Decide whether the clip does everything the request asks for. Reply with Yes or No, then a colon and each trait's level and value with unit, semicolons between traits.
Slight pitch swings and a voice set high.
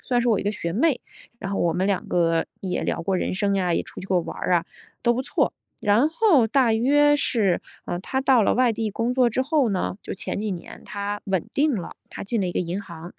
No: average, 5.3 semitones; high, 205 Hz